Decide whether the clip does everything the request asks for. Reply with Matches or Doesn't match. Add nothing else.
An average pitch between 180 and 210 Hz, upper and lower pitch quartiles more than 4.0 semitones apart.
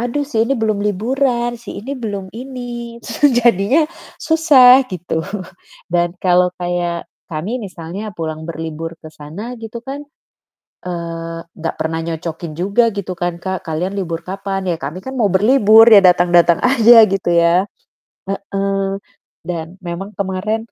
Matches